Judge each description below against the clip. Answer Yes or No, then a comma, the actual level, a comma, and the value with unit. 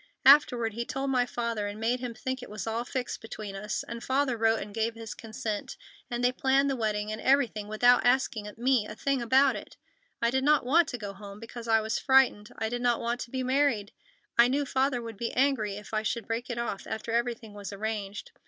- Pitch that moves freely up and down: No, average, 3.1 semitones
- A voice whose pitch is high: Yes, high, 235 Hz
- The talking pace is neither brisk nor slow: No, fast, 225 wpm